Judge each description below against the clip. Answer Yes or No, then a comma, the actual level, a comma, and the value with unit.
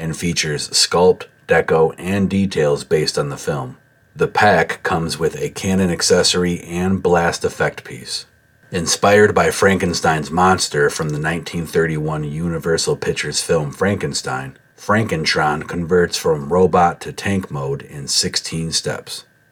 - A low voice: Yes, very low, 85 Hz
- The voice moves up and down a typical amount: Yes, average, 3.0 semitones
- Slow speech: Yes, slow, 130 wpm